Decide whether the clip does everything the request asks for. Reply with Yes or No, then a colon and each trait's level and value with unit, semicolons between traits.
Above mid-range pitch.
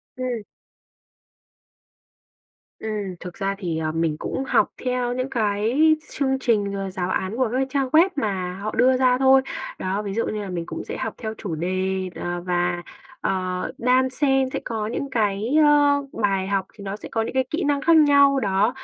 Yes: high, 220 Hz